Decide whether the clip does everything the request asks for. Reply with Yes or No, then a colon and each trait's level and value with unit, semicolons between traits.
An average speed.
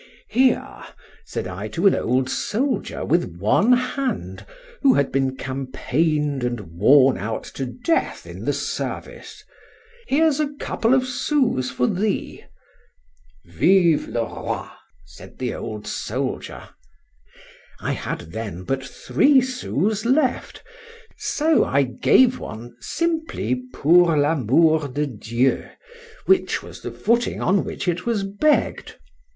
No: slow, 120 wpm